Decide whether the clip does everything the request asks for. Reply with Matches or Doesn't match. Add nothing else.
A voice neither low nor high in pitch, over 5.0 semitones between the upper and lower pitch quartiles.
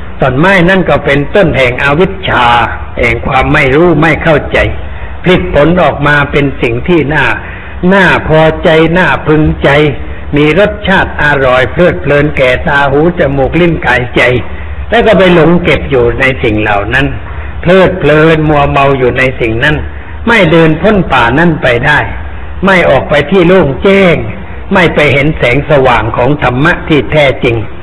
Matches